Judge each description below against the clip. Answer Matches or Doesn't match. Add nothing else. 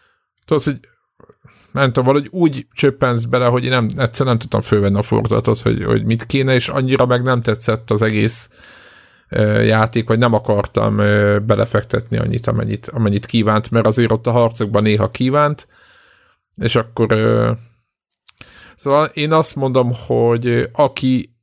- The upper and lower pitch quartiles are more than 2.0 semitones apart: Matches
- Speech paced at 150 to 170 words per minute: Matches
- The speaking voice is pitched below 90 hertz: Doesn't match